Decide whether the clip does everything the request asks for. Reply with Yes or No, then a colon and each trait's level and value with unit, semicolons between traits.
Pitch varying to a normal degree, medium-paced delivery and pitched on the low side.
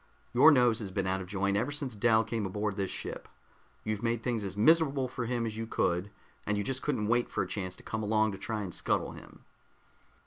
No: average, 3.2 semitones; fast, 235 wpm; low, 110 Hz